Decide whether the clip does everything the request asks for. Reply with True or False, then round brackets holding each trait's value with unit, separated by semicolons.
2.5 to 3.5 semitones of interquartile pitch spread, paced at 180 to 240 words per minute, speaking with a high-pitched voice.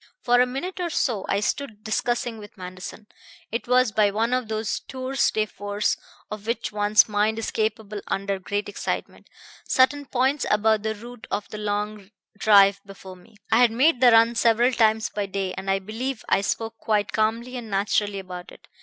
True (2.9 semitones; 190 wpm; 215 Hz)